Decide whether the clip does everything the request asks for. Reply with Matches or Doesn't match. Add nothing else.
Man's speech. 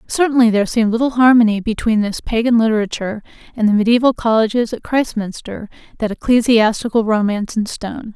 Doesn't match